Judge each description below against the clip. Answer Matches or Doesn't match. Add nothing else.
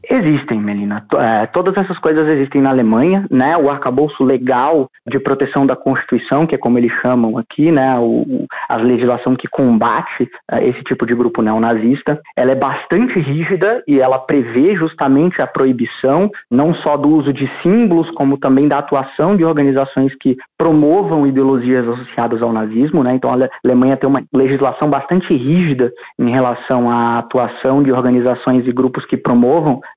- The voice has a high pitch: Doesn't match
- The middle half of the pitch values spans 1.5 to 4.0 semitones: Matches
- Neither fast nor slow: Matches